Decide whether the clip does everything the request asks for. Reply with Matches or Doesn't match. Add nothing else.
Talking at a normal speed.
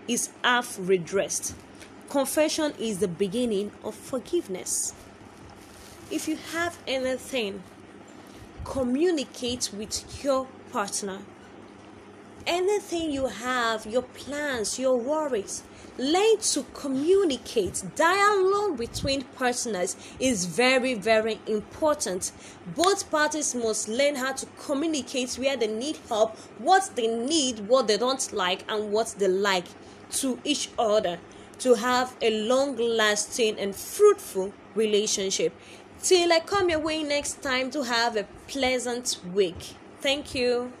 Doesn't match